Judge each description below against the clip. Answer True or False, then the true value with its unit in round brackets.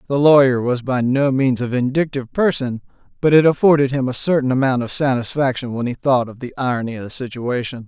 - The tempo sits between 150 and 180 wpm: False (205 wpm)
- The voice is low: True (130 Hz)